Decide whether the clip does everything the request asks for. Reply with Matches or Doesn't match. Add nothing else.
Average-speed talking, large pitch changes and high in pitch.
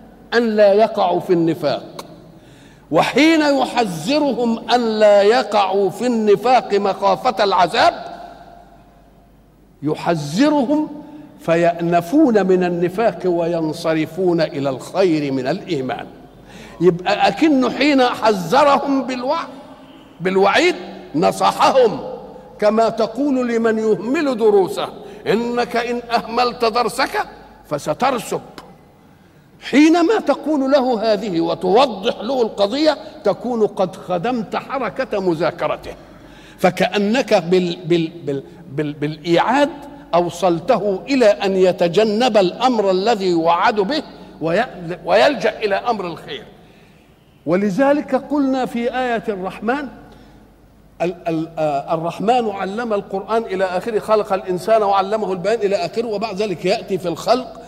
Matches